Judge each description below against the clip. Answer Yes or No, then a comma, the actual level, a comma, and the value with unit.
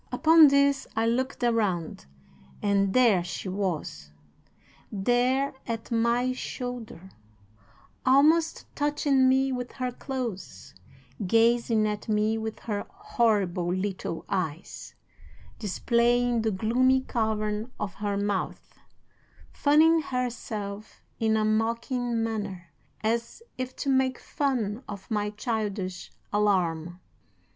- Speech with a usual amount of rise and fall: Yes, average, 3.9 semitones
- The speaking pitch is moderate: No, high, 225 Hz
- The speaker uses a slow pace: Yes, slow, 105 wpm